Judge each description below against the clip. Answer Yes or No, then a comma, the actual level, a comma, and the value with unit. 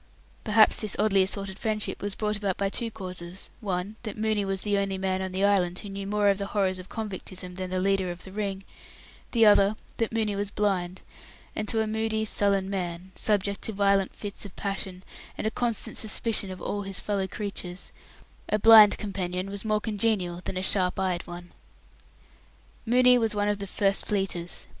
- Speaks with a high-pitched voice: Yes, high, 200 Hz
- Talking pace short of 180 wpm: No, average, 195 wpm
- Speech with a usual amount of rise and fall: No, narrow, 2.0 semitones